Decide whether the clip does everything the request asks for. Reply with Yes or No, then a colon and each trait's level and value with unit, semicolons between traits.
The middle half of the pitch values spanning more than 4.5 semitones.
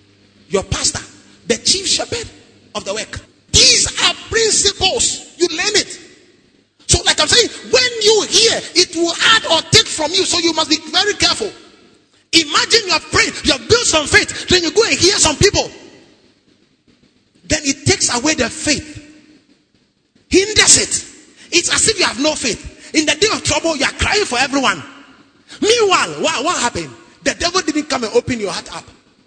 Yes: average, 5.1 semitones